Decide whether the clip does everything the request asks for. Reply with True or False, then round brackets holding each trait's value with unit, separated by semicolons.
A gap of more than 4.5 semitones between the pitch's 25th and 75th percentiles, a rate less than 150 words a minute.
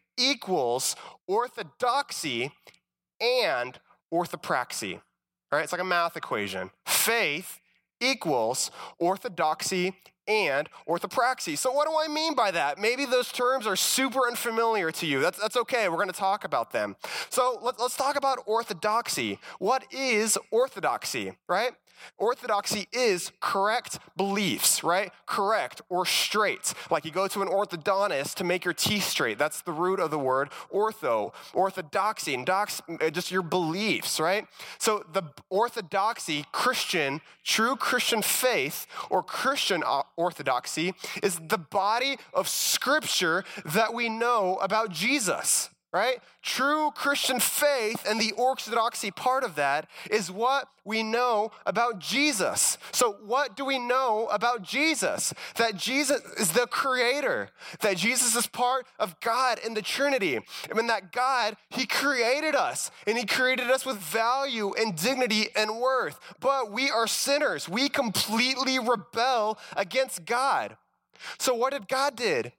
True (5.1 semitones; 140 wpm)